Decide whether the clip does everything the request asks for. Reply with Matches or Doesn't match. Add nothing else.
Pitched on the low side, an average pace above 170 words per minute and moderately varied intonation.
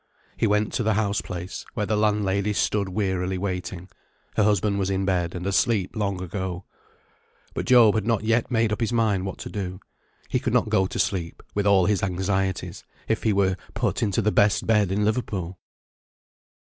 Doesn't match